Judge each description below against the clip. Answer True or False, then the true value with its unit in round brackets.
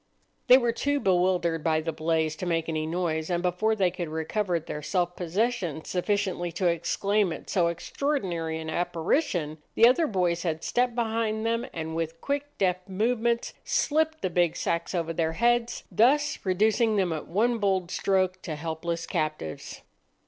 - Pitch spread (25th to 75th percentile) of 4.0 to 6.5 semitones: True (5.1 semitones)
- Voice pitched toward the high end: False (180 Hz)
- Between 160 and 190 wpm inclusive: True (165 wpm)